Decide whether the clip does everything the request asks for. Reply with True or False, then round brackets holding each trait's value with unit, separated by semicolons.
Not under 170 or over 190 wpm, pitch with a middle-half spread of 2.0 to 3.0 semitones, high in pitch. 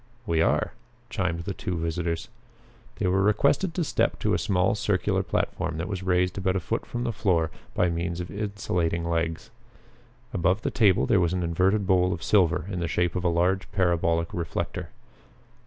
False (185 wpm; 2.5 semitones; 90 Hz)